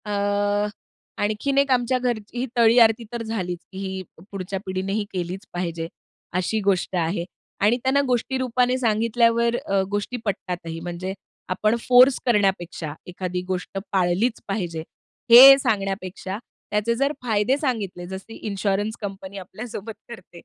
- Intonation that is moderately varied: Yes, average, 4.1 semitones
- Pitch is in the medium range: No, high, 205 Hz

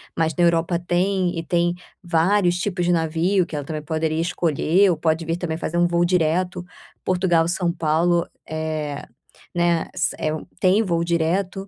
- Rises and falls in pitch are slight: Yes, narrow, 1.8 semitones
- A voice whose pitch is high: No, medium, 170 Hz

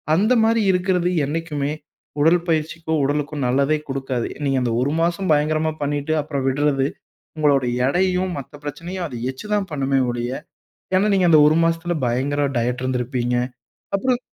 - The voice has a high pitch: No, medium, 150 Hz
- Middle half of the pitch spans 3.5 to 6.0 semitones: Yes, average, 4.2 semitones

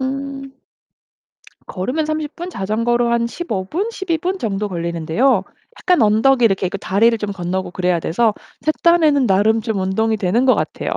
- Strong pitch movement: Yes, wide, 6.2 semitones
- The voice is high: Yes, high, 230 Hz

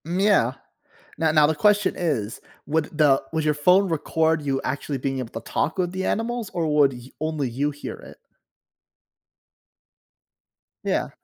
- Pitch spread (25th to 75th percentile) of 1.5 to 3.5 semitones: No, average, 4.3 semitones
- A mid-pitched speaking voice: Yes, medium, 155 Hz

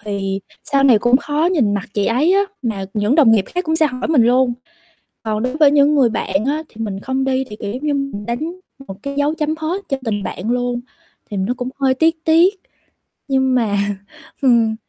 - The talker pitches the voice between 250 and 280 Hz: Yes, very high, 255 Hz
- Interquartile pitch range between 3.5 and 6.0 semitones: Yes, average, 5.3 semitones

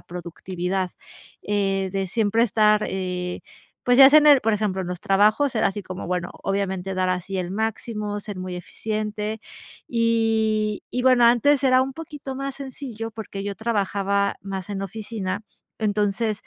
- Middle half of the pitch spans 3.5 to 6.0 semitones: No, average, 3.1 semitones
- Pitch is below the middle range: No, high, 210 Hz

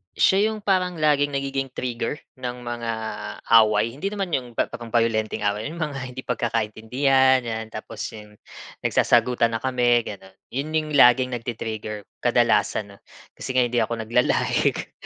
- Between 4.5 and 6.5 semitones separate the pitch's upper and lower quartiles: No, average, 3.6 semitones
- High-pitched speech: No, low, 125 Hz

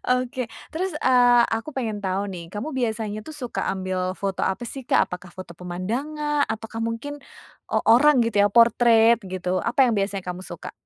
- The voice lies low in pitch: No, high, 225 Hz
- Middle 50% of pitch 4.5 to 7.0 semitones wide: Yes, average, 4.8 semitones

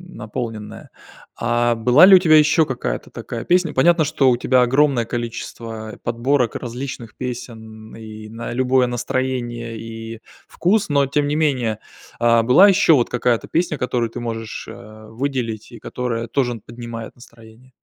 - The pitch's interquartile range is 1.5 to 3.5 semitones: Yes, average, 2.8 semitones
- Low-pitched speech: Yes, low, 120 Hz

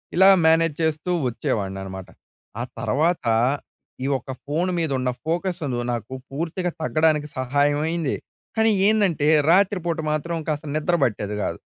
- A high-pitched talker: No, medium, 155 Hz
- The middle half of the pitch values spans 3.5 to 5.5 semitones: Yes, average, 3.9 semitones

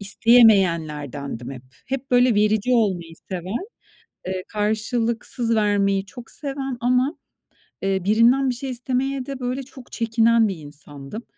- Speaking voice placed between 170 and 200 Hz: No, high, 225 Hz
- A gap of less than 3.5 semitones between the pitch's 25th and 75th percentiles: No, average, 4.6 semitones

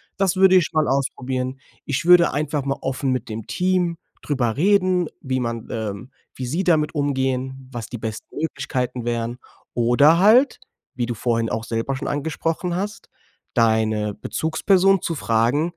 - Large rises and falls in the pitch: Yes, wide, 6.0 semitones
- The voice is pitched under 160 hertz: Yes, low, 135 Hz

